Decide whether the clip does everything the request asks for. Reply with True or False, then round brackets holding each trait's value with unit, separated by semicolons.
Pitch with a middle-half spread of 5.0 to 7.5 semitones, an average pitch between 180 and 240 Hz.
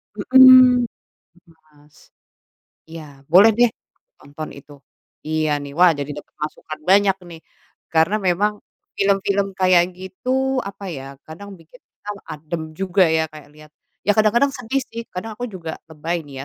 True (5.4 semitones; 185 Hz)